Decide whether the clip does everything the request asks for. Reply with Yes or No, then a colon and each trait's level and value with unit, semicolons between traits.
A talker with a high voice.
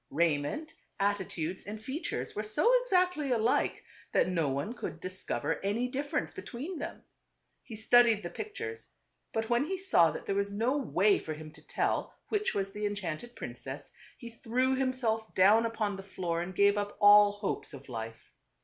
Yes: high, 210 Hz